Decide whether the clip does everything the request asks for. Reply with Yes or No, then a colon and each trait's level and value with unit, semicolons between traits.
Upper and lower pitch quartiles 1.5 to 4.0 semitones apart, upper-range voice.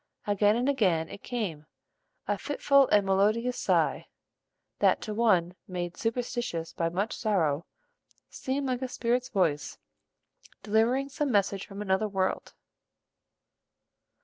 No: average, 4.7 semitones; high, 210 Hz